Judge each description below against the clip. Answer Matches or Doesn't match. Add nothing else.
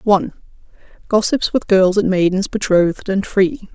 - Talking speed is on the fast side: Doesn't match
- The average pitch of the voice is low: Doesn't match